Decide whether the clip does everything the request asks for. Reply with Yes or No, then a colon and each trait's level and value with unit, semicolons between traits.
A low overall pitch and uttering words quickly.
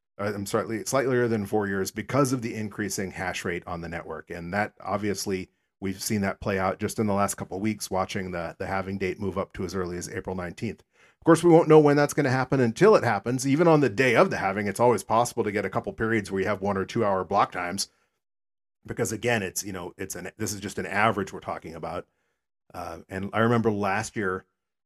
Yes: low, 100 Hz; fast, 250 wpm